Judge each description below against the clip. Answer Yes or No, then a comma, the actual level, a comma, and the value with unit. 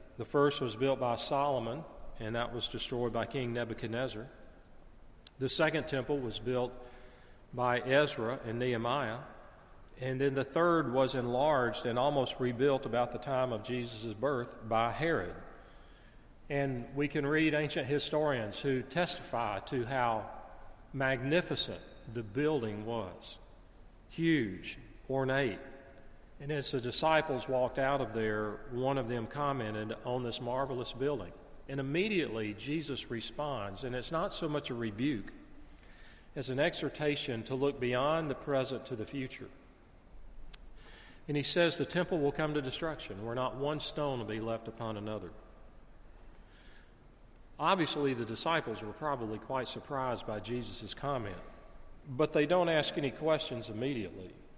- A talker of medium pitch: No, low, 130 Hz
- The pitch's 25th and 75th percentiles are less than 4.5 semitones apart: Yes, average, 3.8 semitones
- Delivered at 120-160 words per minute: Yes, average, 140 wpm